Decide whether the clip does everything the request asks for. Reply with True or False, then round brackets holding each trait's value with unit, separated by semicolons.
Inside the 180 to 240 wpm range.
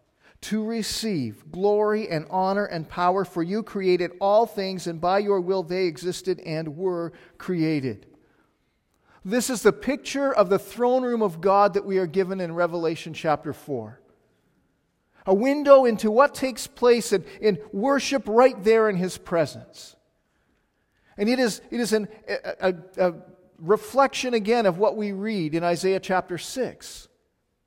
False (155 wpm)